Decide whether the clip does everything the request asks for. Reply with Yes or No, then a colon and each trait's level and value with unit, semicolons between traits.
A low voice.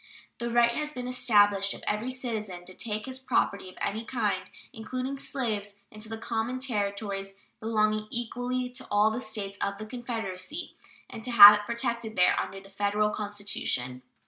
No: high, 215 Hz